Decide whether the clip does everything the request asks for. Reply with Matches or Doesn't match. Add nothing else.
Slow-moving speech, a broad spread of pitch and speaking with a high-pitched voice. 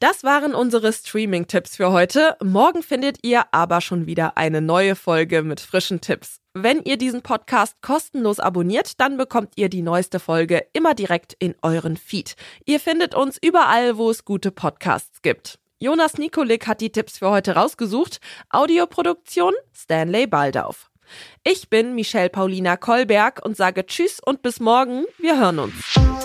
Doesn't match